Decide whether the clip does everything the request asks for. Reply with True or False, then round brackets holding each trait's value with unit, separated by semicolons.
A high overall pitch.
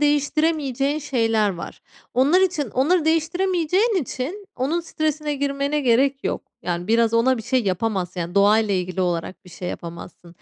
True (265 Hz)